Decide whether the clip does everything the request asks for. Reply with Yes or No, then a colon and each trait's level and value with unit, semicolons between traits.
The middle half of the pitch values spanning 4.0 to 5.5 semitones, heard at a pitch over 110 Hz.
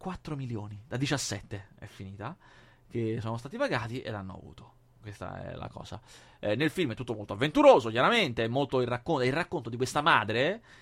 Yes: average, 5.0 semitones; low, 125 Hz